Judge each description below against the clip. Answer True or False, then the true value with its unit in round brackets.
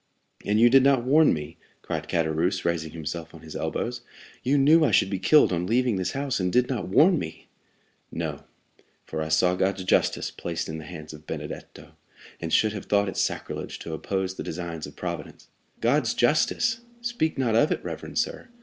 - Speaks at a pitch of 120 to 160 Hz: False (95 Hz)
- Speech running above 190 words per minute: True (200 wpm)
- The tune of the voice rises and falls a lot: True (7.9 semitones)